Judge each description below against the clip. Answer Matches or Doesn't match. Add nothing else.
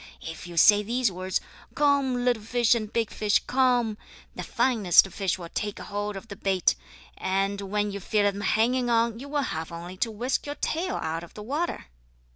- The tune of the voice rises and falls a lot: Doesn't match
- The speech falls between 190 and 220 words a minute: Matches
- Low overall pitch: Doesn't match